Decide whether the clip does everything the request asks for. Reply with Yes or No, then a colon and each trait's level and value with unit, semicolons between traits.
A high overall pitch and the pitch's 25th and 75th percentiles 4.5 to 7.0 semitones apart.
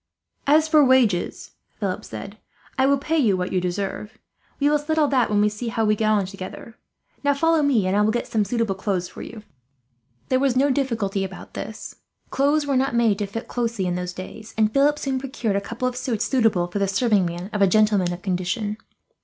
Yes: high, 220 Hz; average, 5.1 semitones